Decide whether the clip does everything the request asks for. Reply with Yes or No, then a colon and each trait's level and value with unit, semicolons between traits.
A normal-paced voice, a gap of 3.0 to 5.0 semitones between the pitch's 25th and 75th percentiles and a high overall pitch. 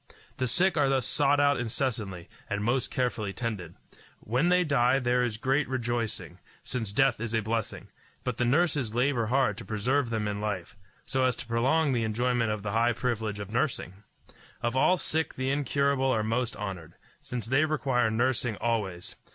No: average, 180 wpm; average, 3.5 semitones; low, 120 Hz